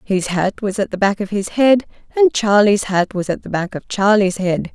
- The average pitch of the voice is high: Yes, high, 205 Hz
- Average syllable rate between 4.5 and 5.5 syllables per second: Yes, 4.8 syllables/s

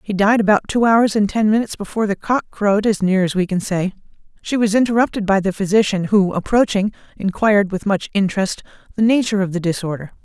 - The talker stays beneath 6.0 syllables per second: No, 6.3 syllables/s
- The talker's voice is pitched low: No, high, 205 Hz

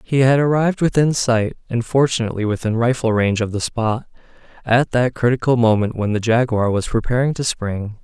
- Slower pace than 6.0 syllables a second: Yes, 5.5 syllables/s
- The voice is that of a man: Yes, male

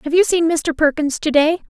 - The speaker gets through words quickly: Yes, fast, 235 wpm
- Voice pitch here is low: No, very high, 315 Hz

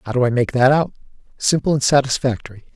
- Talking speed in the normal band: Yes, average, 195 wpm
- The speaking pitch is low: Yes, low, 130 Hz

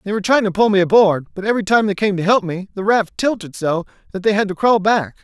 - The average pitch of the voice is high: Yes, high, 200 Hz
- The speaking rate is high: Yes, fast, 285 wpm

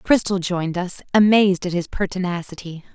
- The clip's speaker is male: No, female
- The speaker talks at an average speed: Yes, average, 145 wpm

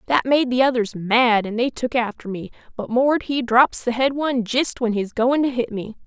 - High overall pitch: Yes, high, 245 Hz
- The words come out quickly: Yes, fast, 235 wpm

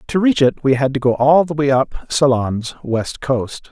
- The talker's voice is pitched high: No, low, 135 Hz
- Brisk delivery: Yes, fast, 225 wpm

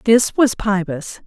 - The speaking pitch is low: No, high, 205 Hz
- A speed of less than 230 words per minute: Yes, average, 140 wpm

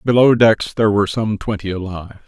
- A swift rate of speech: No, average, 185 wpm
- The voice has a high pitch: No, low, 105 Hz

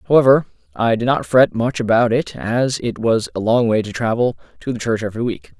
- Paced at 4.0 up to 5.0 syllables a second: No, 5.6 syllables/s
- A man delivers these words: Yes, male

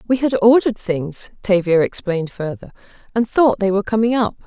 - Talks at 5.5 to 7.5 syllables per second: Yes, 5.7 syllables/s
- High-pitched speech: Yes, high, 205 Hz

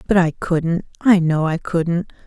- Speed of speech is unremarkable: Yes, average, 185 wpm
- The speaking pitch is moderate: Yes, medium, 175 Hz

